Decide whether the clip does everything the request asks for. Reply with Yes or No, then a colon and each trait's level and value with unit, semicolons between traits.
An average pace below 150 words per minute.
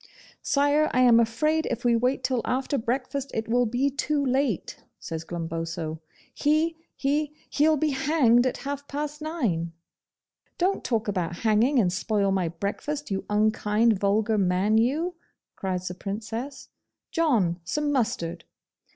Yes: average, 140 wpm